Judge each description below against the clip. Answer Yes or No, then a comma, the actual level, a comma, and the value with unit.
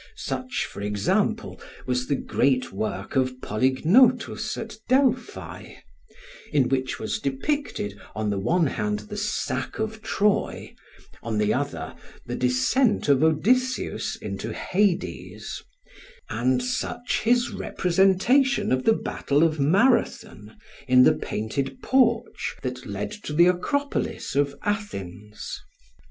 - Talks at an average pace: No, slow, 120 wpm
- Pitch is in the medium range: Yes, medium, 155 Hz